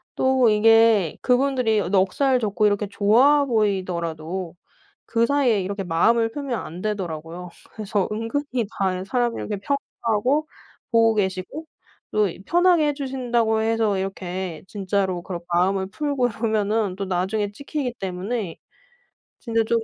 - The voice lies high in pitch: Yes, high, 215 Hz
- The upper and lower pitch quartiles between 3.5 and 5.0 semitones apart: Yes, average, 4.4 semitones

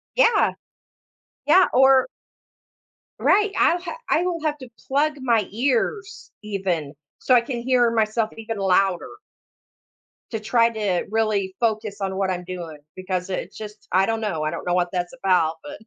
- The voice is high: Yes, high, 215 Hz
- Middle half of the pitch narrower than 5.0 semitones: No, wide, 5.4 semitones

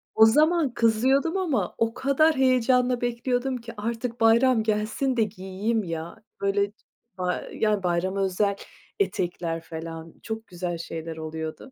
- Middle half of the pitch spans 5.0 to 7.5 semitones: Yes, wide, 5.6 semitones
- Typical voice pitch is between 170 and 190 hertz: No, high, 220 Hz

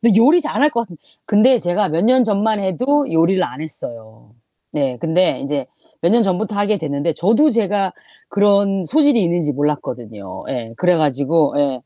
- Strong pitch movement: Yes, wide, 7.0 semitones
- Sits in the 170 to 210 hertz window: Yes, medium, 185 Hz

